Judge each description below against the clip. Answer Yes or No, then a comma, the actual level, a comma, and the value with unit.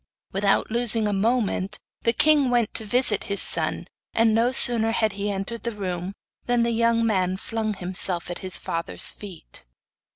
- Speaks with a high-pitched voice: Yes, high, 215 Hz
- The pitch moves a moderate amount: Yes, average, 3.3 semitones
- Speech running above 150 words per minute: Yes, average, 170 wpm